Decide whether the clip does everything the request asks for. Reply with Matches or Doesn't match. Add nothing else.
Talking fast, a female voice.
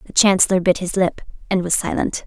Matches